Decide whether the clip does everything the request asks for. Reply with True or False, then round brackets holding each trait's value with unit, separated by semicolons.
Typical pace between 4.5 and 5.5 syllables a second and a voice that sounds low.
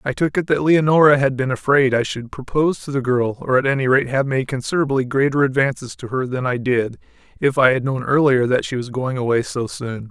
False (5.7 syllables/s; 130 Hz)